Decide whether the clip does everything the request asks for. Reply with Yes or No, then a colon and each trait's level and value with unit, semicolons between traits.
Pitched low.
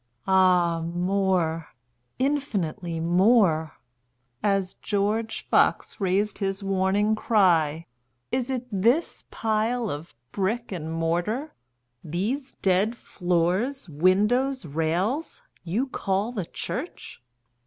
No: high, 190 Hz